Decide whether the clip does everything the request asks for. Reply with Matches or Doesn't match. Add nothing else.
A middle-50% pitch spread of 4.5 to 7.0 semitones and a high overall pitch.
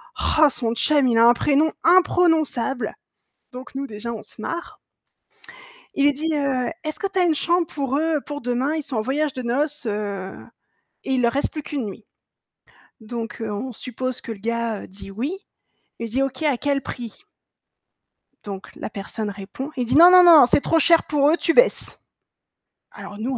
Matches